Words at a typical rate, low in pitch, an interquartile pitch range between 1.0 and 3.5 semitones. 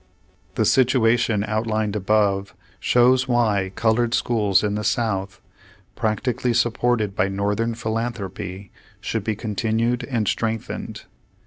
No: slow, 110 wpm; low, 110 Hz; narrow, 2.6 semitones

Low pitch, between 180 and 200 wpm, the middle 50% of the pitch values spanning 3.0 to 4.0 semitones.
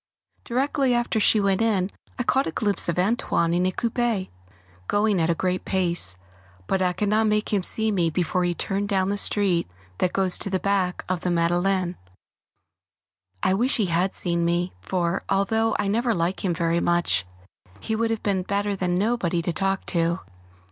No: high, 190 Hz; average, 190 wpm; average, 3.3 semitones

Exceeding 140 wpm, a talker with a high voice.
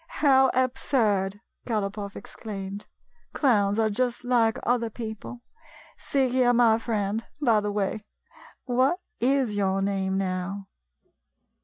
No: slow, 135 wpm; high, 220 Hz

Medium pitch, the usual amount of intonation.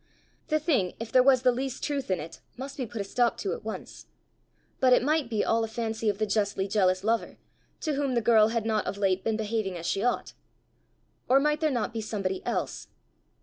No: high, 225 Hz; average, 4.0 semitones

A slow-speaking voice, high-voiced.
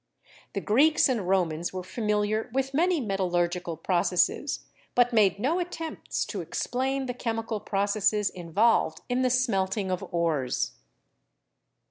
Yes: slow, 125 wpm; high, 210 Hz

